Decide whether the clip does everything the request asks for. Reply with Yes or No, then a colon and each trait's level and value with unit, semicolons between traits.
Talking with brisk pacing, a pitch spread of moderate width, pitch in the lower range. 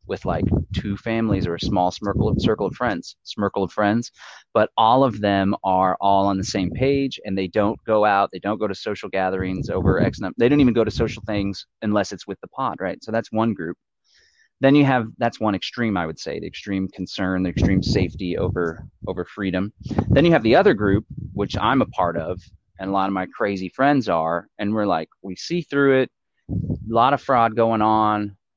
Yes: fast, 225 wpm; average, 3.1 semitones; low, 100 Hz